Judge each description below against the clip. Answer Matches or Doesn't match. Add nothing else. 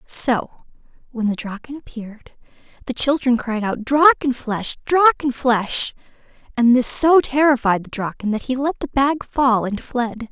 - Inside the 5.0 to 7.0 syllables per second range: Doesn't match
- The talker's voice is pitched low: Doesn't match